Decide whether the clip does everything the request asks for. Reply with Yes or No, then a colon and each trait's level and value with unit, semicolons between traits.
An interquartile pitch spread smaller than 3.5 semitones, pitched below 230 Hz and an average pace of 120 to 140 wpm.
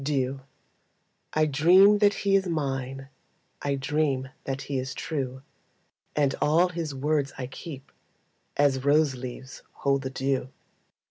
Yes: average, 2.8 semitones; medium, 140 Hz; slow, 135 wpm